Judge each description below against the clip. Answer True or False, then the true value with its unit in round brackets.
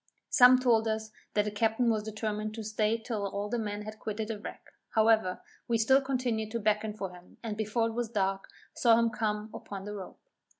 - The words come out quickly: True (210 wpm)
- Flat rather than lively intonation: True (1.5 semitones)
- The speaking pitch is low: False (220 Hz)